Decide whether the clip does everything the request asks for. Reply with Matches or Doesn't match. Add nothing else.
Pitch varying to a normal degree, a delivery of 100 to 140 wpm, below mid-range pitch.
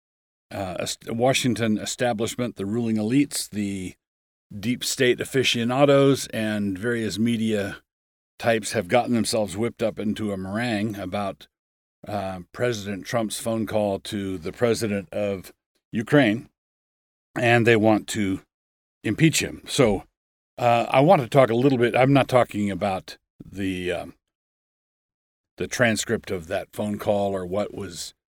Matches